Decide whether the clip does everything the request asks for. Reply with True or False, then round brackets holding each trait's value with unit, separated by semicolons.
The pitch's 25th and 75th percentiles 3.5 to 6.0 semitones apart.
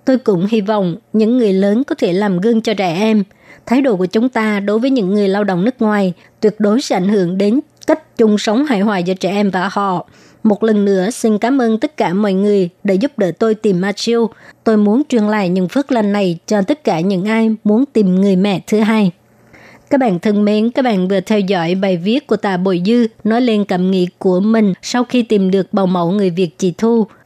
False (2.9 semitones)